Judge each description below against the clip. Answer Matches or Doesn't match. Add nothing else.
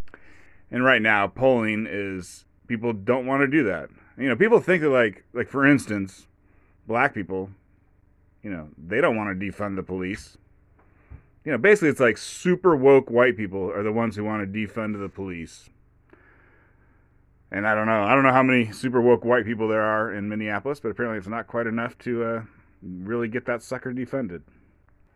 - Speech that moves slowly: Doesn't match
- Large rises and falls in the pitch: Doesn't match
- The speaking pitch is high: Doesn't match